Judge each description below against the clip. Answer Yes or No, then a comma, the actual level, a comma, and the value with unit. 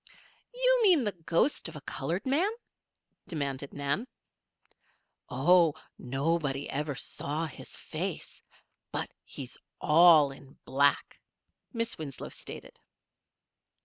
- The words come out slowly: Yes, slow, 105 wpm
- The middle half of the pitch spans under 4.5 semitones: No, average, 5.2 semitones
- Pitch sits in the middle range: Yes, medium, 155 Hz